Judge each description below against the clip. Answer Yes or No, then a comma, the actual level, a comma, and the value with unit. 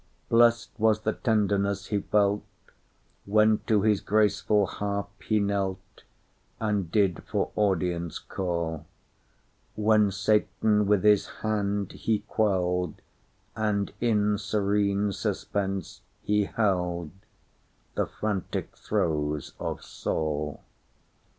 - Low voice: Yes, low, 100 Hz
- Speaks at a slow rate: Yes, slow, 85 wpm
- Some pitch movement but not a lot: No, narrow, 2.1 semitones